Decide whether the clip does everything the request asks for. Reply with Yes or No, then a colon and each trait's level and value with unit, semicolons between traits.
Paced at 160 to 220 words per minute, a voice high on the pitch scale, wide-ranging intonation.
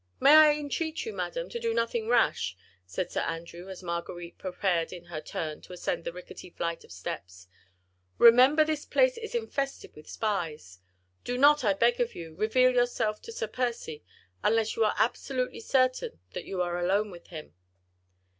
Yes: average, 175 wpm; high, 215 Hz; wide, 7.5 semitones